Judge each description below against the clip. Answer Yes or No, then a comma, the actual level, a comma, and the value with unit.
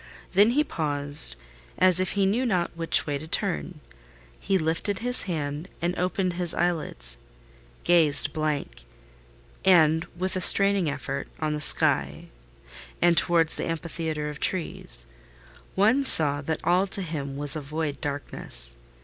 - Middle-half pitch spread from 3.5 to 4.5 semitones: Yes, average, 4.0 semitones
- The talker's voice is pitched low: No, medium, 165 Hz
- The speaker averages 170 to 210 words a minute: No, average, 140 wpm